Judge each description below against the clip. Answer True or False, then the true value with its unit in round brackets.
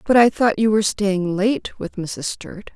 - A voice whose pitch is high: True (205 Hz)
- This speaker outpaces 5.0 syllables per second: False (4.2 syllables/s)